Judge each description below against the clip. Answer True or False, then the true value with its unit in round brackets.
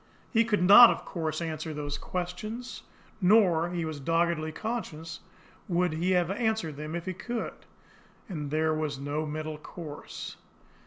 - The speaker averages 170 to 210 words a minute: False (150 wpm)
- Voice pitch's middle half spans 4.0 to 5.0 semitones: False (3.2 semitones)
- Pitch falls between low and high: True (170 Hz)